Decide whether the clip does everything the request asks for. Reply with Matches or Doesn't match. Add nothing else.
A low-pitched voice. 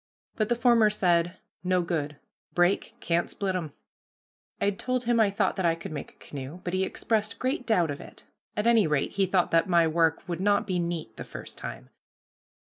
Doesn't match